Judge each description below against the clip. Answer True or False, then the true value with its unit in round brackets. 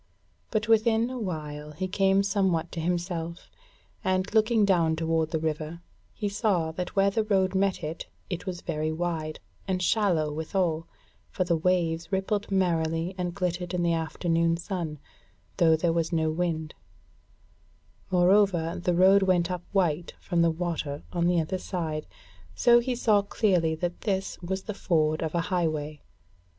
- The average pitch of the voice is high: False (175 Hz)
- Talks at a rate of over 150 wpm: True (160 wpm)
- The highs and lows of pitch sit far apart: False (3.0 semitones)